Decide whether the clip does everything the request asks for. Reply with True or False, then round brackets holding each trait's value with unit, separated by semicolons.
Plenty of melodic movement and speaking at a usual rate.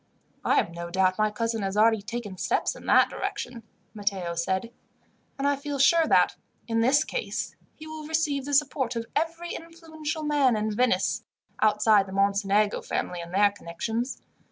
True (6.4 semitones; 170 wpm)